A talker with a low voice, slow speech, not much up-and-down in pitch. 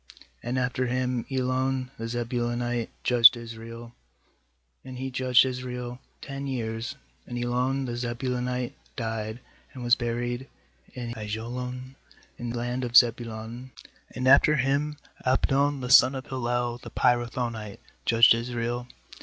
Yes: low, 125 Hz; slow, 130 wpm; narrow, 1.4 semitones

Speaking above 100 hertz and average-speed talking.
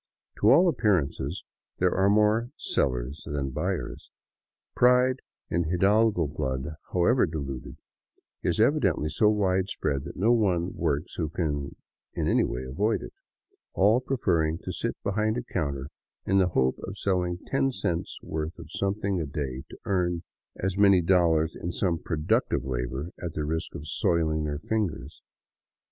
No: very low, 85 Hz; average, 150 wpm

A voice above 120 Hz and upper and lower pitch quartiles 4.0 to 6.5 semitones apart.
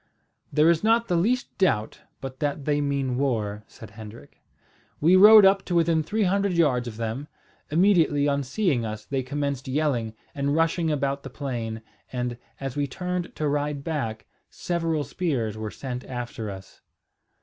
Yes: medium, 140 Hz; wide, 5.4 semitones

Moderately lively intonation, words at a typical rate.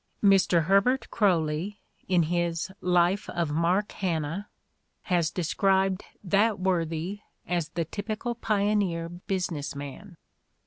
No: average, 3.2 semitones; slow, 105 wpm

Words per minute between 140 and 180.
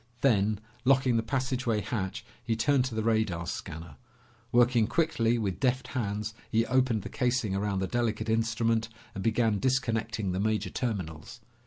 Yes: average, 155 wpm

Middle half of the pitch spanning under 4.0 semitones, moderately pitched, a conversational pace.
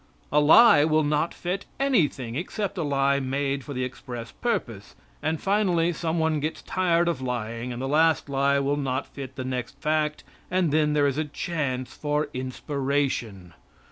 Yes: average, 3.6 semitones; medium, 145 Hz; average, 175 wpm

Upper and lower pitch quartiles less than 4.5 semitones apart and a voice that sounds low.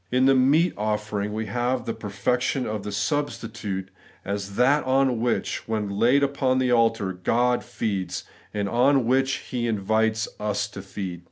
Yes: average, 3.8 semitones; low, 115 Hz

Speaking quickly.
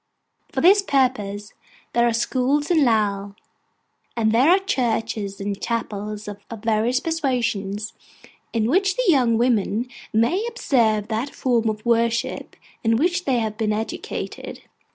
No: slow, 135 wpm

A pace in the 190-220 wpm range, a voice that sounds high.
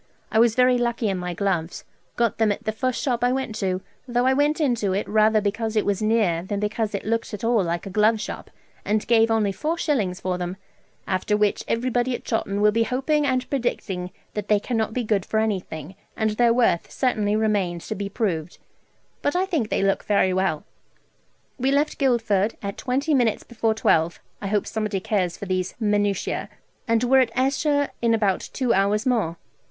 Yes: average, 200 wpm; high, 220 Hz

